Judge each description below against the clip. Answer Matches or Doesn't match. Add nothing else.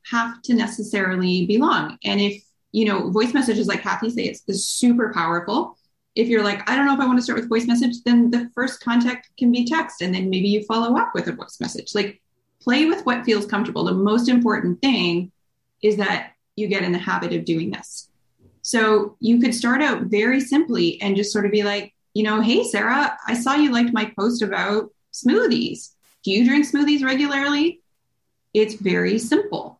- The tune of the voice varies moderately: Matches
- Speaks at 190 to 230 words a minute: Matches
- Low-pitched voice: Doesn't match